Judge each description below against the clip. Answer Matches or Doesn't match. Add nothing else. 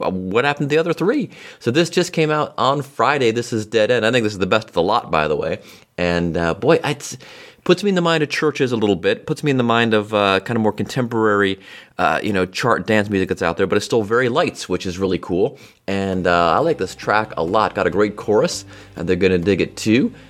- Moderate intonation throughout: Doesn't match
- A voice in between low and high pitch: Doesn't match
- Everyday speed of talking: Doesn't match